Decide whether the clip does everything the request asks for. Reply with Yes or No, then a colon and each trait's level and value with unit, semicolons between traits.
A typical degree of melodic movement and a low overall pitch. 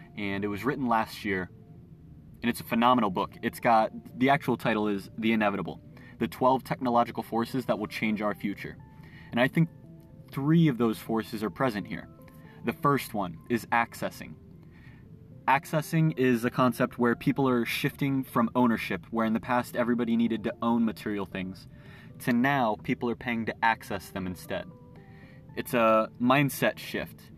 Yes: average, 3.0 semitones; low, 120 Hz